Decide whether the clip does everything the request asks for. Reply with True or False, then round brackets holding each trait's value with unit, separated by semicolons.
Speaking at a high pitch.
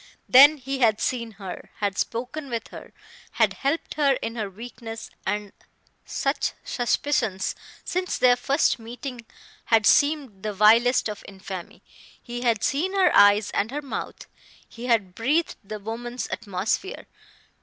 True (235 Hz)